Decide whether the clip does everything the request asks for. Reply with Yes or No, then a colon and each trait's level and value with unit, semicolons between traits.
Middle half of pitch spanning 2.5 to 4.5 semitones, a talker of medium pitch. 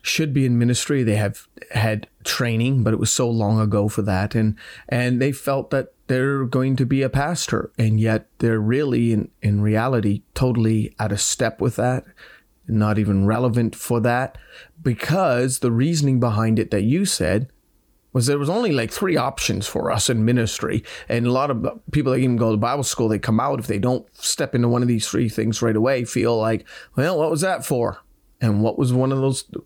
No: average, 3.0 semitones; low, 120 Hz